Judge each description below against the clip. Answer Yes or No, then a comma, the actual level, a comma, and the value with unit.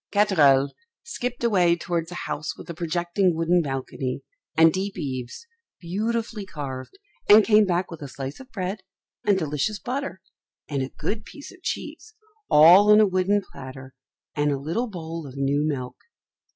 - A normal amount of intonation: No, wide, 6.2 semitones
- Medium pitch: Yes, medium, 175 Hz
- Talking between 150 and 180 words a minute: Yes, average, 165 wpm